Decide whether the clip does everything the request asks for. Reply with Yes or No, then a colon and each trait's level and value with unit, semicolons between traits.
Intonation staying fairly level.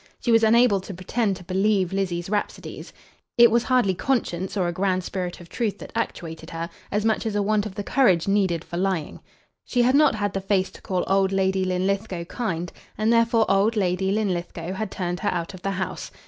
No: average, 3.0 semitones